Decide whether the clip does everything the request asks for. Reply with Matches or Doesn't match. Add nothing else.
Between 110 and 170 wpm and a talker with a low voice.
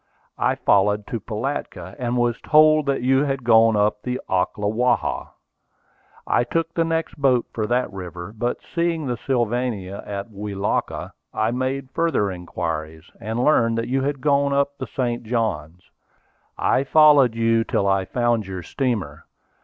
Matches